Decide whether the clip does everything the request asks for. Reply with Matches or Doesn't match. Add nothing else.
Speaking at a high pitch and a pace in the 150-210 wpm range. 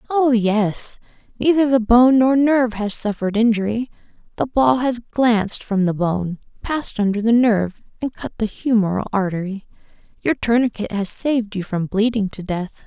Matches